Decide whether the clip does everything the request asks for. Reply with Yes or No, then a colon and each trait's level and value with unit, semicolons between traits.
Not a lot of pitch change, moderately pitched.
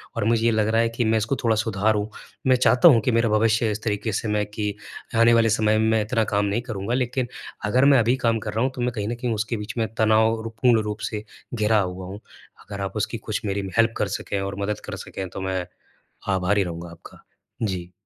No: narrow, 2.0 semitones; low, 110 Hz